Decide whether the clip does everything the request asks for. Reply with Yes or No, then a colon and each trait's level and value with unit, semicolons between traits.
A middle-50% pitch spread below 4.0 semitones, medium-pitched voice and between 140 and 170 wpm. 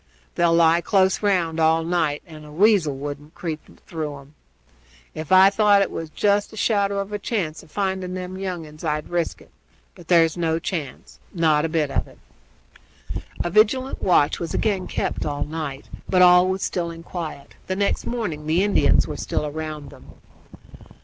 No: average, 3.6 semitones; medium, 170 Hz; average, 185 wpm